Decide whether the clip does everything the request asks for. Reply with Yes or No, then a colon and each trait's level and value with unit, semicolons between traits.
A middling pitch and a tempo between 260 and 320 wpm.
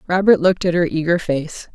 No: medium, 170 Hz; fast, 205 wpm